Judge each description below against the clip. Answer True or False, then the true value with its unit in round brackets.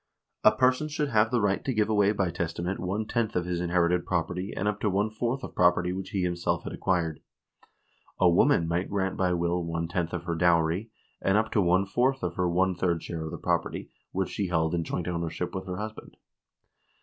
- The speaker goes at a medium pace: False (220 wpm)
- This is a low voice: True (90 Hz)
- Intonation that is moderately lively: True (3.1 semitones)